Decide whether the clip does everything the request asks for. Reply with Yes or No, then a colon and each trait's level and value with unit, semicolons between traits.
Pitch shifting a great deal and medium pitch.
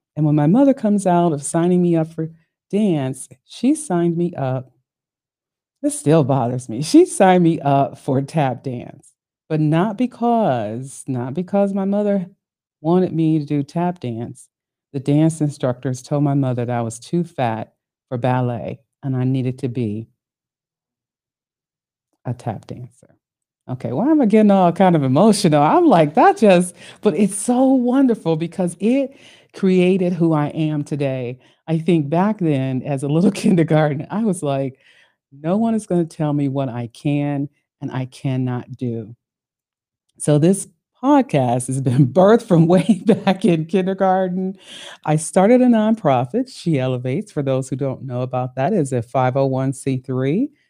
Yes: wide, 6.3 semitones; medium, 155 Hz